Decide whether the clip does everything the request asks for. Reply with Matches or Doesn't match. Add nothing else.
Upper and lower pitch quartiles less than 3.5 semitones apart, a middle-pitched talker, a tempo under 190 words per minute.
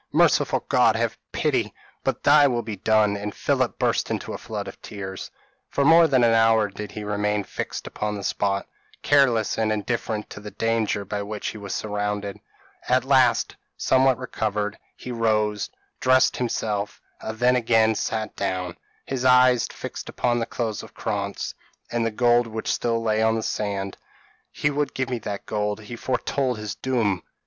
Doesn't match